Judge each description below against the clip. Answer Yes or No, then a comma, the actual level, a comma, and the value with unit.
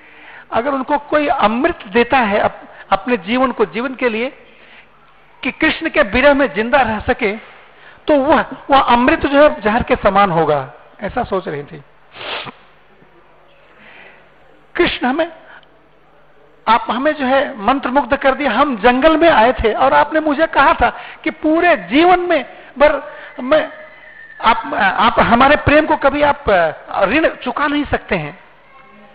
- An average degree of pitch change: Yes, average, 4.1 semitones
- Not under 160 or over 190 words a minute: No, average, 150 wpm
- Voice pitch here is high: Yes, very high, 275 Hz